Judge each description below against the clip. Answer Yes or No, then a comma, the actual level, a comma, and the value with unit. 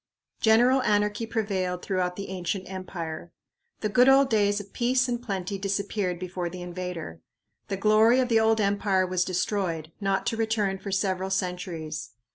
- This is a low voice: No, high, 195 Hz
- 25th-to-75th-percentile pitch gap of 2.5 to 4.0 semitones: Yes, average, 3.2 semitones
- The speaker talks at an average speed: Yes, average, 160 wpm